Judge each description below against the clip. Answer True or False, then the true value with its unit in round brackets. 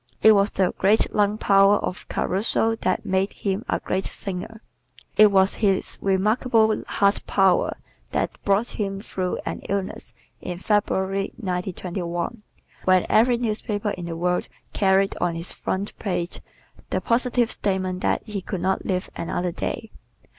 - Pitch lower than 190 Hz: False (195 Hz)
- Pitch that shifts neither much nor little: False (2.3 semitones)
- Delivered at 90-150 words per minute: True (145 wpm)